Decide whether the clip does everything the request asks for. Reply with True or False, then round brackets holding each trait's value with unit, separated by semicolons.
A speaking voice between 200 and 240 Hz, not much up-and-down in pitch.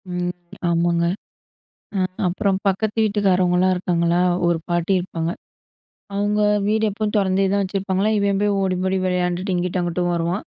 False (185 Hz; 2.2 semitones)